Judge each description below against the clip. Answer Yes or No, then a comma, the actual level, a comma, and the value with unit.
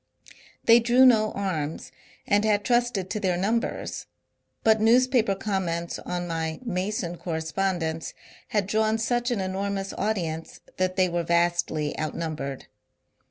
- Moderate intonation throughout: Yes, average, 4.3 semitones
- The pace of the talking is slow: Yes, slow, 125 wpm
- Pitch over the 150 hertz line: Yes, high, 190 Hz